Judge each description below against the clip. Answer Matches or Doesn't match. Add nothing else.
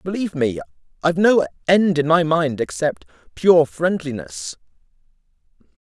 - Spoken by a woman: Doesn't match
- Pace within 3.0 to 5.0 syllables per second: Matches